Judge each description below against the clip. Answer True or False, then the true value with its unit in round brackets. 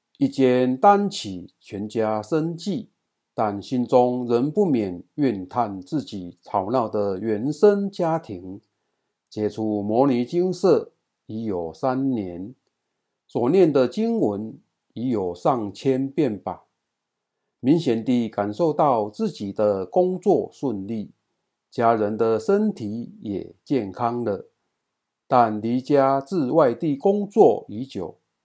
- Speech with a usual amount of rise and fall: False (7.4 semitones)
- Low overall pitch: True (120 Hz)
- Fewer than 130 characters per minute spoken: False (165 characters per minute)